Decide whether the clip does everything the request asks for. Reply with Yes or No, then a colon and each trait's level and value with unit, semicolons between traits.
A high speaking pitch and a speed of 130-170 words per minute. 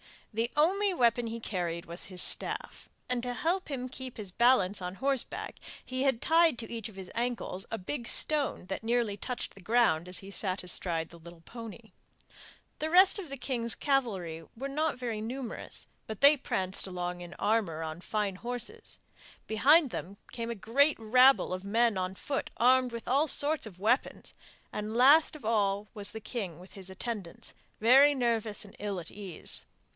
No: high, 230 Hz; average, 185 wpm